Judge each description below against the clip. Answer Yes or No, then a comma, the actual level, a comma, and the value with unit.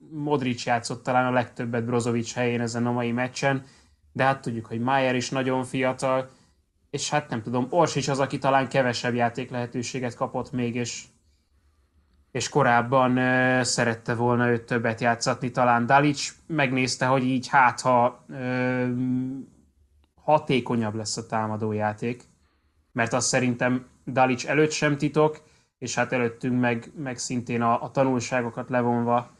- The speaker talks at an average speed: Yes, average, 145 wpm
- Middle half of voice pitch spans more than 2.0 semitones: No, narrow, 1.7 semitones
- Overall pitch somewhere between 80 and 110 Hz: No, low, 125 Hz